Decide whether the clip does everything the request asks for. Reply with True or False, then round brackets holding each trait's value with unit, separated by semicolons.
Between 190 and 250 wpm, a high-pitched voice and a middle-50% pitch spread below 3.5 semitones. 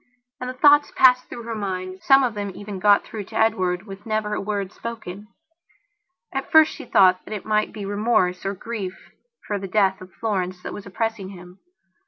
True (200 wpm; 205 Hz; 3.1 semitones)